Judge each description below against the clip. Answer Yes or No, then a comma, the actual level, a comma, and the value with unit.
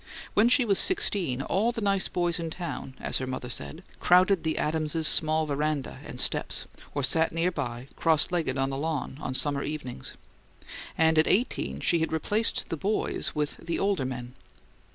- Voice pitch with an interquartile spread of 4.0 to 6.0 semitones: Yes, average, 4.6 semitones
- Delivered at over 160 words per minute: Yes, average, 180 wpm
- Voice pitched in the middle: Yes, medium, 160 Hz